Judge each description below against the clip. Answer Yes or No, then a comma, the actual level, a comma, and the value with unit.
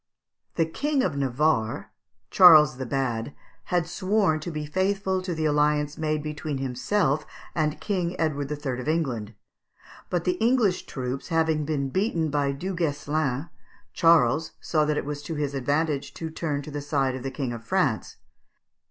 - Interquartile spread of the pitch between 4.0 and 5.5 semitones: No, average, 3.3 semitones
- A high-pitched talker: No, medium, 150 Hz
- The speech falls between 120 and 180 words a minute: Yes, average, 165 wpm